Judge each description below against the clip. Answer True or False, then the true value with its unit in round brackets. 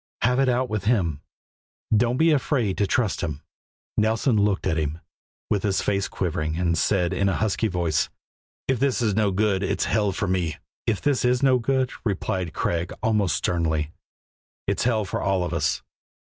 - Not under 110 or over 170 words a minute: False (180 wpm)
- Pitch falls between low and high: False (100 Hz)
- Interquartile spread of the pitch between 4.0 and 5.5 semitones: True (4.9 semitones)